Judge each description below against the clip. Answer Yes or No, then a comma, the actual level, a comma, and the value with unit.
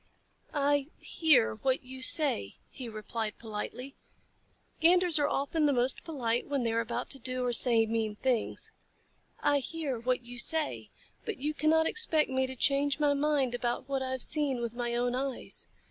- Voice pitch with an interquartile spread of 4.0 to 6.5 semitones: No, average, 3.4 semitones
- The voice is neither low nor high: No, very high, 260 Hz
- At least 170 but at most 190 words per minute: Yes, average, 175 wpm